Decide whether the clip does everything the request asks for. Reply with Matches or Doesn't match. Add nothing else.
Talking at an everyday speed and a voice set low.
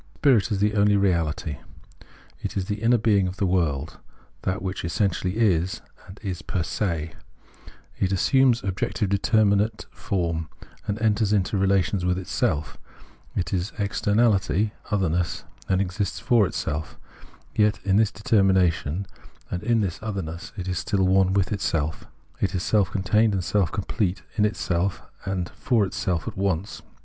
Matches